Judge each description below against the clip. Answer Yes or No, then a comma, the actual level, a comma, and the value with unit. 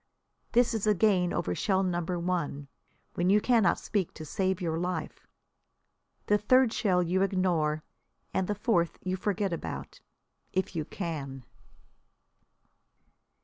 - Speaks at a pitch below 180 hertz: No, medium, 185 Hz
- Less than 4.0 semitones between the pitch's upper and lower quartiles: Yes, average, 3.3 semitones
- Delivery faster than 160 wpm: No, slow, 135 wpm